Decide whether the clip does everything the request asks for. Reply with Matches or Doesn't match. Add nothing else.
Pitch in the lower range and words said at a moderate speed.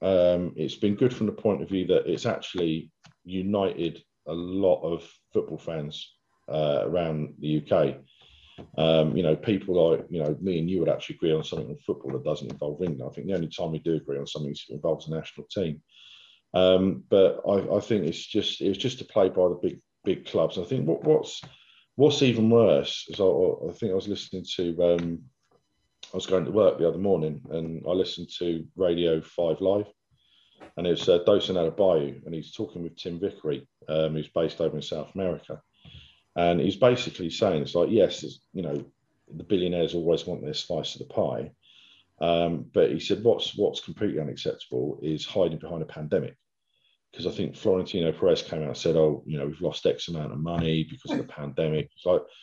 Doesn't match